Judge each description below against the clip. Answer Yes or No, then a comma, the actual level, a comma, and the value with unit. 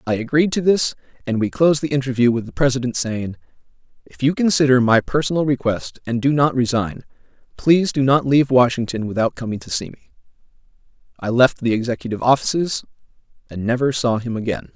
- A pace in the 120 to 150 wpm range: No, average, 175 wpm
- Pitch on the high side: No, low, 130 Hz